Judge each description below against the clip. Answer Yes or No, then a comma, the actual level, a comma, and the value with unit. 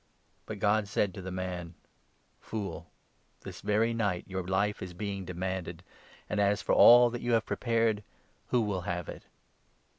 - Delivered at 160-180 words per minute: Yes, average, 175 wpm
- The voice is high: No, low, 100 Hz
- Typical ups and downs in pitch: Yes, average, 3.0 semitones